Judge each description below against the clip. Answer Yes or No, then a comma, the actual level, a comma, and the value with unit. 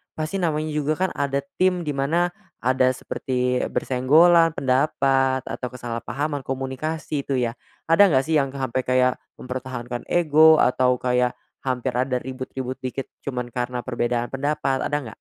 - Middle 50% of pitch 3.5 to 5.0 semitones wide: No, average, 3.0 semitones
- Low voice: Yes, low, 130 Hz